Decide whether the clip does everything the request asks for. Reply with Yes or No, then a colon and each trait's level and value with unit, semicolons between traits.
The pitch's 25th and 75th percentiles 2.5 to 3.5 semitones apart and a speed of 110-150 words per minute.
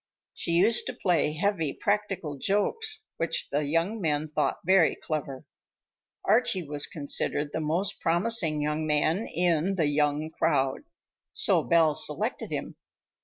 No: average, 4.4 semitones; slow, 135 wpm